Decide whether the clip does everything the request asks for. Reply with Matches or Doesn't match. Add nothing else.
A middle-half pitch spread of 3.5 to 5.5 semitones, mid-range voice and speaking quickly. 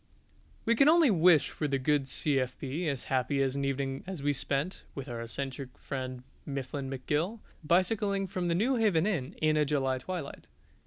Doesn't match